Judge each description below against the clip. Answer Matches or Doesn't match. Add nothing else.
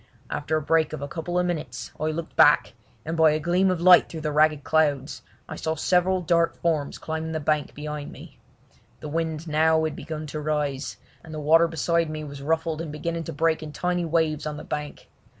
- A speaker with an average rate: Doesn't match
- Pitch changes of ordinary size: Doesn't match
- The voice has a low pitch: Doesn't match